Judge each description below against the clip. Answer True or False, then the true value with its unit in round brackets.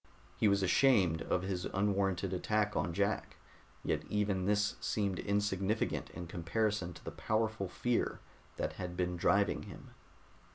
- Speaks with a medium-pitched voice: False (100 Hz)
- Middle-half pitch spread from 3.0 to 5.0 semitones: False (2.5 semitones)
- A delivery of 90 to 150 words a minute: True (140 wpm)